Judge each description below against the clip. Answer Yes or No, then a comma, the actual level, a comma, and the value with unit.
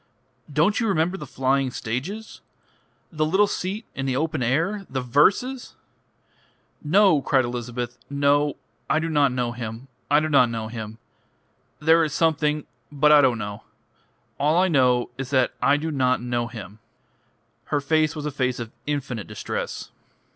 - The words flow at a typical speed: Yes, average, 160 wpm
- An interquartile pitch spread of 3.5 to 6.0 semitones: Yes, average, 4.2 semitones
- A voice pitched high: No, medium, 140 Hz